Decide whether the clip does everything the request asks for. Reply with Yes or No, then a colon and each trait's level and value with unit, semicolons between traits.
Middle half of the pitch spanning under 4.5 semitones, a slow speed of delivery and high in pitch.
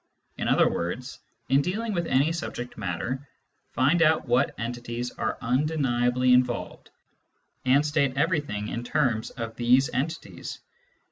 No: average, 3.6 semitones; slow, 130 wpm; low, 130 Hz